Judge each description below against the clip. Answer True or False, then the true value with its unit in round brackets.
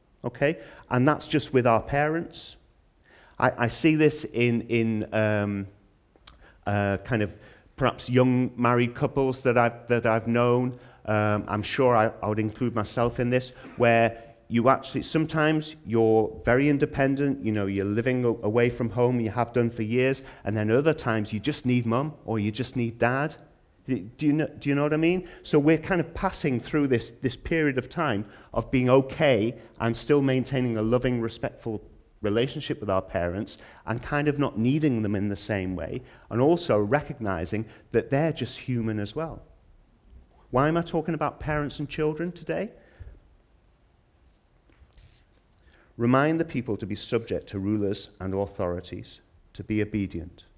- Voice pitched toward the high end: False (120 Hz)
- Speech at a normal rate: True (170 wpm)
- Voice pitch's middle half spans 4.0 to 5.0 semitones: True (4.6 semitones)